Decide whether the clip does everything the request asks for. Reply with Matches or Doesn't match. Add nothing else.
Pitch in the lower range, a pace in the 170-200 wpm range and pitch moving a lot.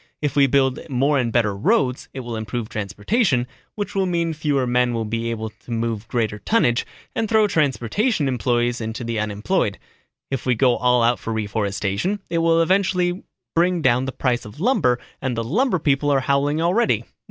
Matches